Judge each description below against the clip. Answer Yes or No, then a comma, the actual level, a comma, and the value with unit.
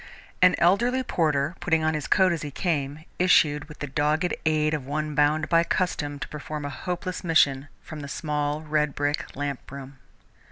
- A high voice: No, medium, 150 Hz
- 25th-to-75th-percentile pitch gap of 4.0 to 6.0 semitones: No, narrow, 2.4 semitones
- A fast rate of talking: No, average, 175 wpm